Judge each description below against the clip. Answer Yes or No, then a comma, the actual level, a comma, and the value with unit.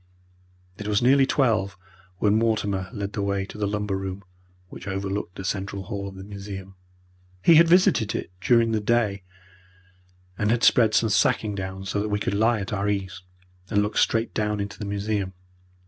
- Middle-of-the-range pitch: No, low, 105 Hz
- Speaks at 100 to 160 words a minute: No, average, 180 wpm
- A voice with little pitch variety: Yes, narrow, 1.9 semitones